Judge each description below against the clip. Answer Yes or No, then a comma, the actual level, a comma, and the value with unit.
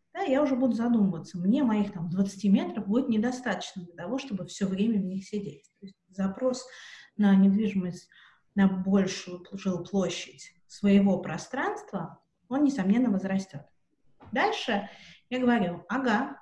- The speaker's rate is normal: Yes, average, 135 wpm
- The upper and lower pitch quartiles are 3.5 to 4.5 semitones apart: Yes, average, 4.0 semitones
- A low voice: No, high, 200 Hz